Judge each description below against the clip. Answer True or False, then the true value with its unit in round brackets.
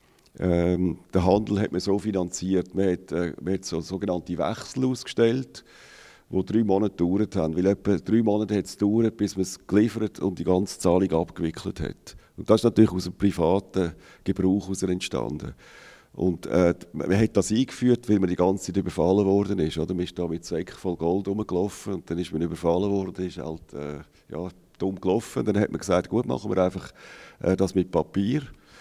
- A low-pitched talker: True (95 Hz)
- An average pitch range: False (2.3 semitones)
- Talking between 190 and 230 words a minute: True (195 wpm)